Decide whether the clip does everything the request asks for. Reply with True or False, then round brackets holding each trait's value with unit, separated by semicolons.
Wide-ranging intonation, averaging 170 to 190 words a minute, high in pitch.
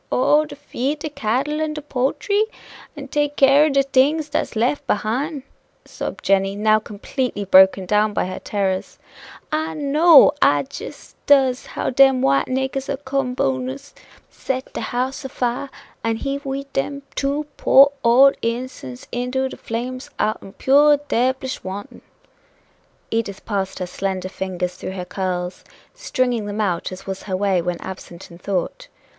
False (6.2 semitones; 160 wpm; 250 Hz)